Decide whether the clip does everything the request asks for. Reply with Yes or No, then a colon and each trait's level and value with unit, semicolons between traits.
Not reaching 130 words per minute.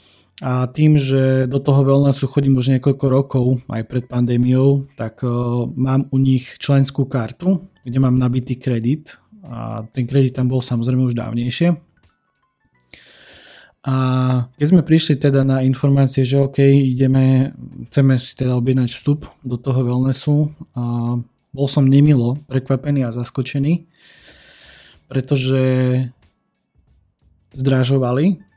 Yes: average, 120 wpm